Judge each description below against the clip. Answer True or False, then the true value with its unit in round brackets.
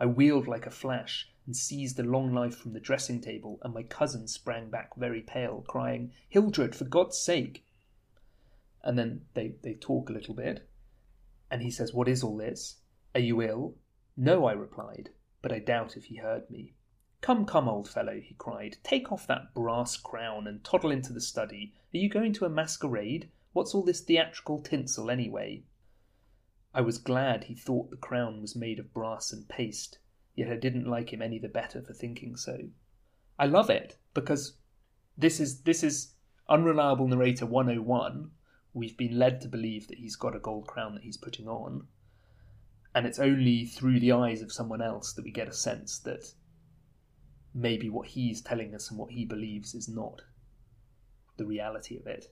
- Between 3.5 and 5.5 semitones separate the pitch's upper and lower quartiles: False (3.0 semitones)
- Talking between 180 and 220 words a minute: True (185 wpm)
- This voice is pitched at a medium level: False (120 Hz)